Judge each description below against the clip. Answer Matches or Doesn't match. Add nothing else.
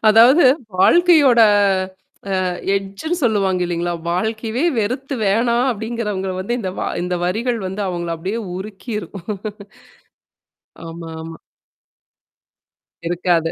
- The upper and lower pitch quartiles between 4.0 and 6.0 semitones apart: Matches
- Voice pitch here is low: Doesn't match